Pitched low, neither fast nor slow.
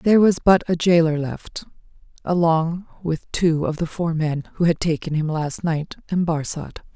No: medium, 165 Hz; average, 180 wpm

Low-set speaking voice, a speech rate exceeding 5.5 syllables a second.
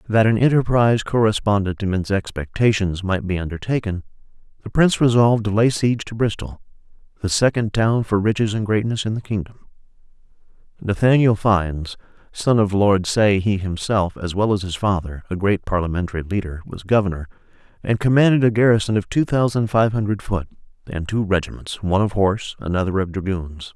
Yes: low, 105 Hz; 5.7 syllables/s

